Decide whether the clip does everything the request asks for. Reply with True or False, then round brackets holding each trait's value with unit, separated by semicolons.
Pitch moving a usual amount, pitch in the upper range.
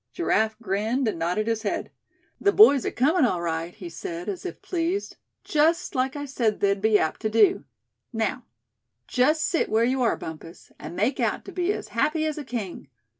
False (6.9 semitones; 230 Hz)